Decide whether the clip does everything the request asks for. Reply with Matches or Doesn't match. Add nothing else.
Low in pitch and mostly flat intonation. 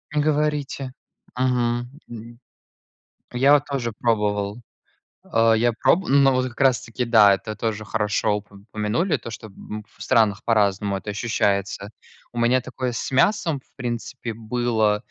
Doesn't match